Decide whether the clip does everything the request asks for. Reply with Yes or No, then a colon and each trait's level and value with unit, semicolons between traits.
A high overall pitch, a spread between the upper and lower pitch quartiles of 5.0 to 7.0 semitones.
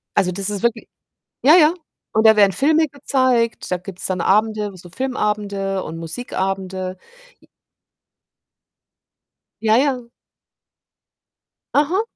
Yes: high, 210 Hz; average, 5.3 semitones